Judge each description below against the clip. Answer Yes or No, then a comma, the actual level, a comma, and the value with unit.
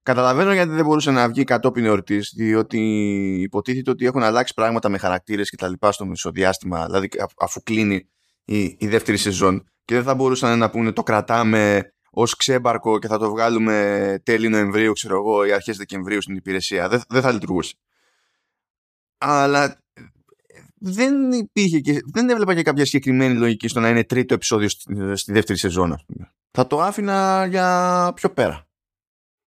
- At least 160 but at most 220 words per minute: Yes, fast, 170 wpm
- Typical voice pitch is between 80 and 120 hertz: Yes, low, 110 Hz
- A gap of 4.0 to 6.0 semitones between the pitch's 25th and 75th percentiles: Yes, average, 4.7 semitones